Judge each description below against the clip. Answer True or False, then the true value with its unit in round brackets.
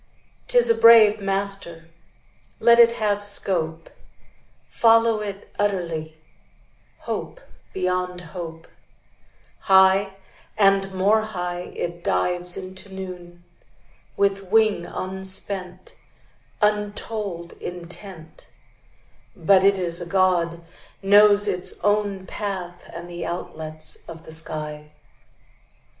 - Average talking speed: False (95 wpm)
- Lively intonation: False (2.8 semitones)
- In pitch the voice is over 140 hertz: True (190 Hz)